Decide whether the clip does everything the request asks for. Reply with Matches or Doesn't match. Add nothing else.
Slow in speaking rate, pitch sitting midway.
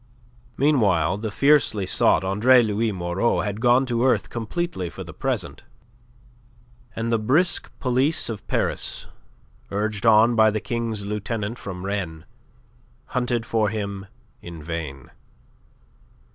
Doesn't match